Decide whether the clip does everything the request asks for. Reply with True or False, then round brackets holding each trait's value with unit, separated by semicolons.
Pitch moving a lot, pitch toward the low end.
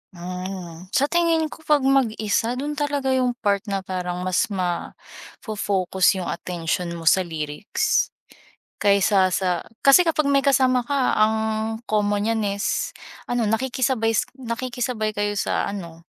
False (5.8 semitones; 215 Hz)